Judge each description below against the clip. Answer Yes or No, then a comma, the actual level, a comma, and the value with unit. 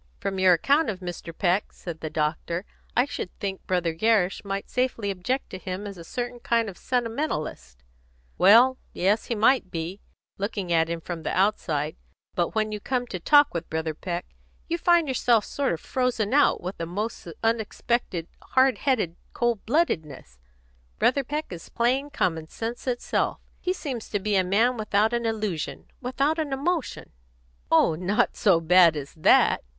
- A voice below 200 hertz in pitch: No, high, 205 Hz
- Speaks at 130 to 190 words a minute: Yes, average, 170 wpm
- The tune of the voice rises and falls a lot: Yes, wide, 6.2 semitones